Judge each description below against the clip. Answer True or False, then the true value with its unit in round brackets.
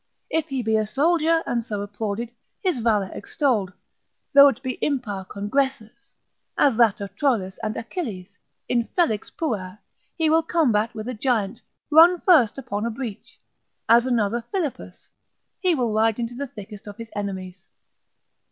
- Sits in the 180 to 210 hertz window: False (230 Hz)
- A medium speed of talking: True (150 wpm)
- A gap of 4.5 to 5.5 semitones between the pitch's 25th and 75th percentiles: True (5.2 semitones)